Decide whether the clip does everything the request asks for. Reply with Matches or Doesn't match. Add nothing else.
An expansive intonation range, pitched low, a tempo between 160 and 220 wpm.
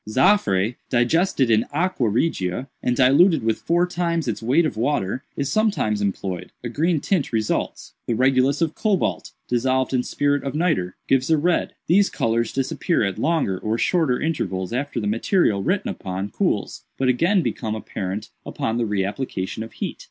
Matches